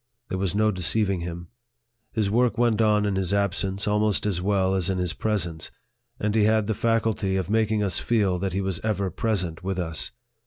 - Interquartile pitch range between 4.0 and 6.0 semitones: No, narrow, 2.6 semitones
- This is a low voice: Yes, low, 100 Hz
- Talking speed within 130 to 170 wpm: No, average, 200 wpm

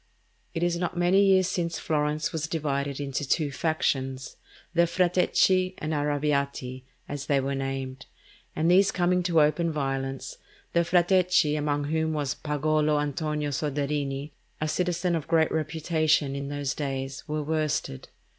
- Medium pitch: Yes, medium, 150 Hz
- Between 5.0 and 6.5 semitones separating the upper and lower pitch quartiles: No, average, 3.2 semitones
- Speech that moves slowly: No, average, 145 wpm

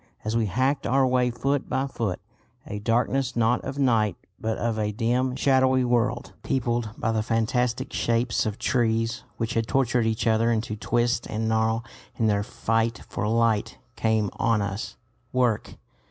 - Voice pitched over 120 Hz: No, low, 115 Hz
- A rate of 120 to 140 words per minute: No, average, 165 wpm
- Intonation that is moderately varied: No, narrow, 2.1 semitones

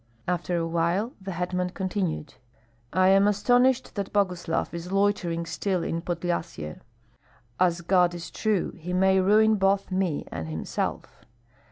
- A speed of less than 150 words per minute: Yes, average, 140 wpm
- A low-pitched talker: No, medium, 180 Hz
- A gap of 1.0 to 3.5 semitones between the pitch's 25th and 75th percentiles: Yes, narrow, 2.6 semitones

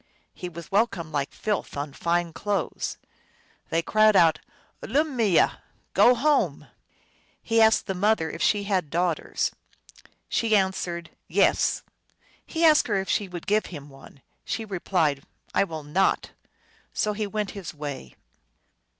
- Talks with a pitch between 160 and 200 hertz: Yes, high, 190 Hz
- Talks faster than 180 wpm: No, average, 160 wpm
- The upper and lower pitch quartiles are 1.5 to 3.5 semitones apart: No, average, 4.8 semitones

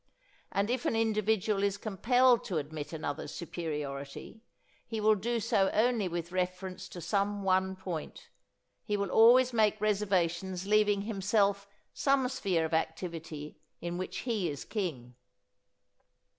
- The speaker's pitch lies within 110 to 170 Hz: No, high, 195 Hz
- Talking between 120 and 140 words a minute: Yes, slow, 135 wpm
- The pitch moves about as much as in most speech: Yes, average, 3.9 semitones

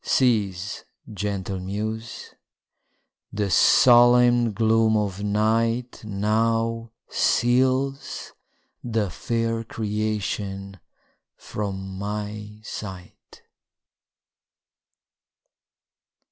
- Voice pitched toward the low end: Yes, low, 110 Hz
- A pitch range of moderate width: No, narrow, 2.3 semitones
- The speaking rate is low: Yes, slow, 60 wpm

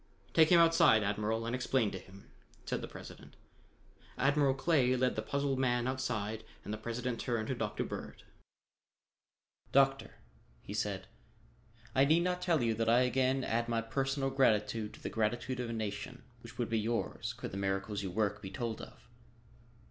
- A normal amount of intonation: Yes, average, 3.7 semitones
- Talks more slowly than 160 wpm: No, average, 175 wpm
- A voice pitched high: No, low, 120 Hz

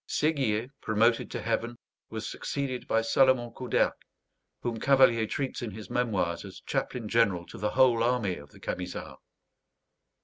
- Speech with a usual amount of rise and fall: Yes, average, 3.0 semitones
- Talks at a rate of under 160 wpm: Yes, average, 145 wpm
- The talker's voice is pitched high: No, low, 115 Hz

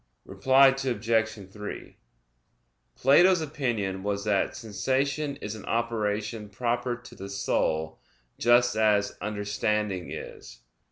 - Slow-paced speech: Yes, slow, 105 wpm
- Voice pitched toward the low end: Yes, low, 110 Hz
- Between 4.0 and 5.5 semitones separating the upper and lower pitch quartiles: No, average, 3.2 semitones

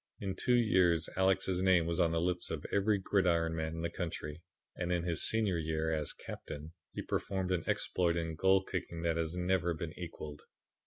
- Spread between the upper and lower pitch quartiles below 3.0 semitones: Yes, narrow, 2.4 semitones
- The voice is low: Yes, very low, 85 Hz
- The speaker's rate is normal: Yes, average, 195 wpm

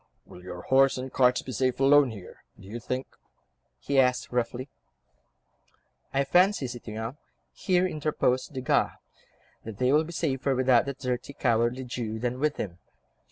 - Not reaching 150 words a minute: No, average, 155 wpm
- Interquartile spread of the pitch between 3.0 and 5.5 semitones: No, narrow, 2.5 semitones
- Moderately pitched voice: No, low, 130 Hz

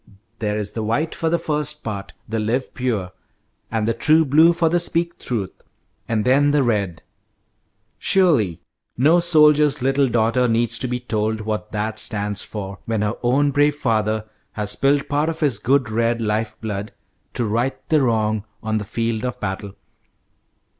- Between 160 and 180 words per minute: Yes, average, 170 wpm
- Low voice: Yes, low, 115 Hz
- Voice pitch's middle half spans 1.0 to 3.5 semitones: No, average, 5.1 semitones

